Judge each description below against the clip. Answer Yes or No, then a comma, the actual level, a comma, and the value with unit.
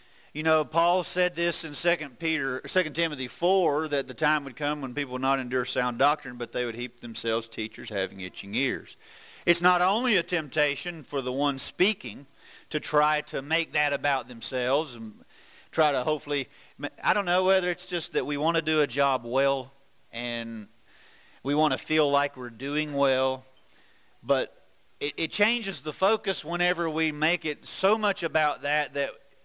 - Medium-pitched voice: Yes, medium, 150 Hz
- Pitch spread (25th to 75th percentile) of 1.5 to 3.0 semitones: No, average, 4.0 semitones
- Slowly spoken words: No, average, 180 wpm